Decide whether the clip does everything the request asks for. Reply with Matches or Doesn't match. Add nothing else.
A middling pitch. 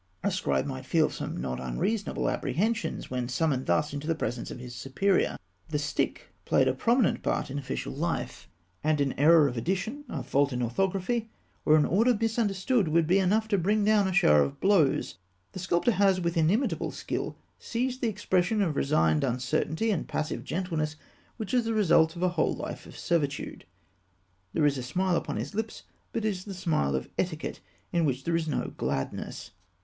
Matches